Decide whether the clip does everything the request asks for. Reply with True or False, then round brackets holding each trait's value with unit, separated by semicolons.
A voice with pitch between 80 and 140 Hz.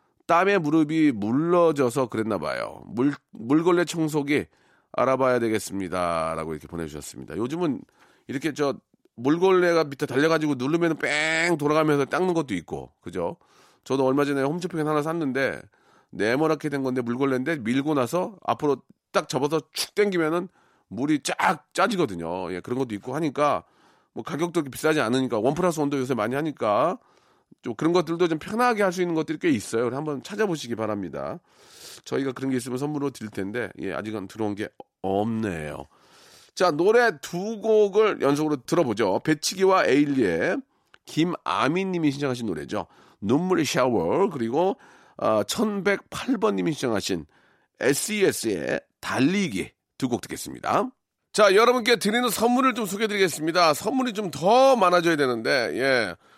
False (150 Hz)